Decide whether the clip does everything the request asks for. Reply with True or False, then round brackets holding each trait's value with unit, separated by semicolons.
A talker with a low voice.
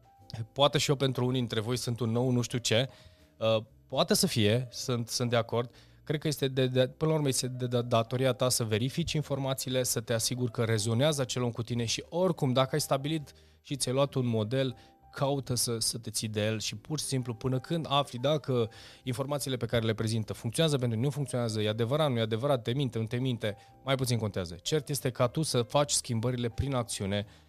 True (125 Hz)